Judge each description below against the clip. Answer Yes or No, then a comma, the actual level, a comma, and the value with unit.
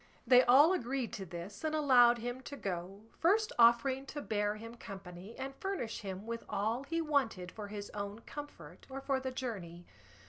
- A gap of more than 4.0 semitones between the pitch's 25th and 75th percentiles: Yes, average, 5.0 semitones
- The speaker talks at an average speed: Yes, average, 180 wpm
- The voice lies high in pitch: Yes, high, 235 Hz